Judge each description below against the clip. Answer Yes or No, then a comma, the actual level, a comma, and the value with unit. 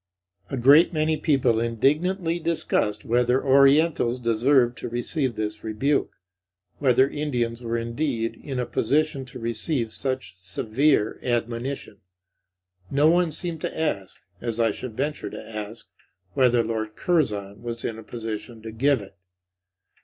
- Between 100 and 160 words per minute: Yes, average, 140 wpm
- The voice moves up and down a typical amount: Yes, average, 4.2 semitones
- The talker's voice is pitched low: Yes, low, 120 Hz